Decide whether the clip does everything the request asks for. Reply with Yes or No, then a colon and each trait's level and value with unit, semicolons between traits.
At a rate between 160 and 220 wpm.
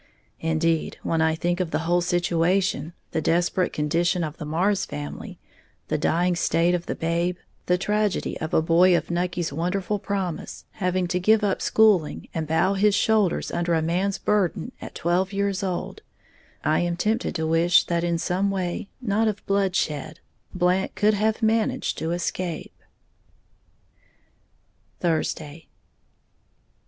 No: average, 145 wpm